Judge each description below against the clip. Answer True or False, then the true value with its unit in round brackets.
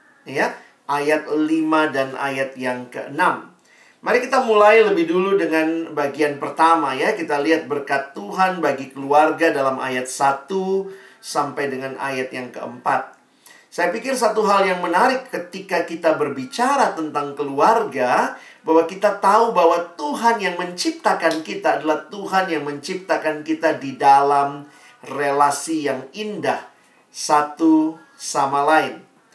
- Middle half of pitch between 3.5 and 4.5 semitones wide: False (5.0 semitones)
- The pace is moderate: True (125 wpm)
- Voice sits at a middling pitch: True (160 Hz)